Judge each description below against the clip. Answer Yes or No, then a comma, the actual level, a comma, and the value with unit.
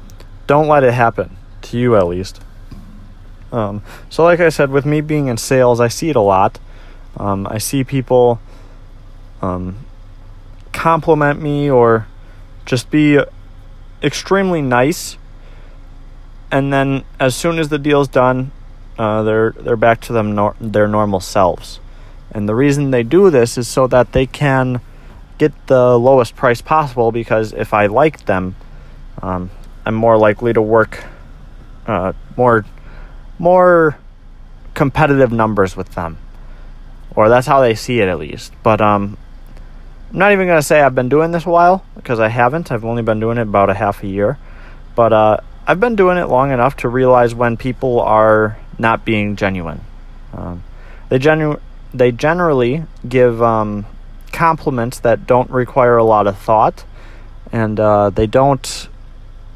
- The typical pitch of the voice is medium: No, low, 120 Hz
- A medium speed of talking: Yes, average, 160 wpm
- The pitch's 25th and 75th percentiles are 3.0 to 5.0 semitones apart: Yes, average, 4.4 semitones